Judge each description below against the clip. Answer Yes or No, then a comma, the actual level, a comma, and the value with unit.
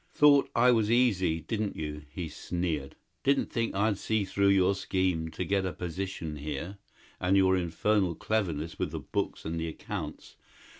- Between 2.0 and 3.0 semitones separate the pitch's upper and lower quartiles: No, average, 4.0 semitones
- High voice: No, very low, 95 Hz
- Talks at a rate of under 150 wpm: No, average, 165 wpm